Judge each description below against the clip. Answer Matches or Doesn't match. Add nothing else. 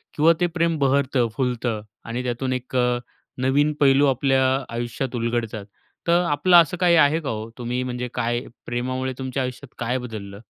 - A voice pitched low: Matches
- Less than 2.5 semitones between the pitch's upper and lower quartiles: Doesn't match